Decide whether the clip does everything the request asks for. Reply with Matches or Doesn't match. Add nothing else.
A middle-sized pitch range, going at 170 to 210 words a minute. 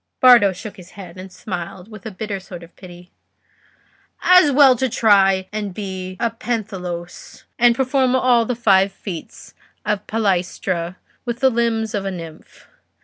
Doesn't match